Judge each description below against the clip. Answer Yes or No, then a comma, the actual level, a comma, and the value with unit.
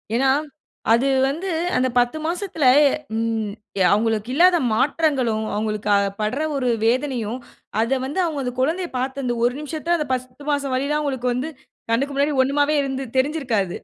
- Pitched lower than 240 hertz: No, very high, 265 Hz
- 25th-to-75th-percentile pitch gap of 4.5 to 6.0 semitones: No, average, 3.5 semitones